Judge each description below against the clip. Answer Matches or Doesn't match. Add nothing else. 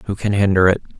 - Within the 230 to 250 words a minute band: Matches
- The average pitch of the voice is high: Doesn't match